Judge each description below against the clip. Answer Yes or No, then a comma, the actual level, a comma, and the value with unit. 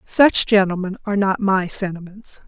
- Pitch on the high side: Yes, high, 195 Hz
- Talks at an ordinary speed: Yes, average, 145 wpm